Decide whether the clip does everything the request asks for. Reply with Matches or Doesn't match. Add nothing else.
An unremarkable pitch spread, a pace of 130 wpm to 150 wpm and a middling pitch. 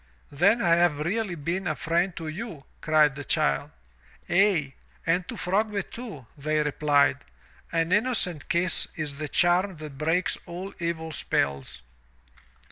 Matches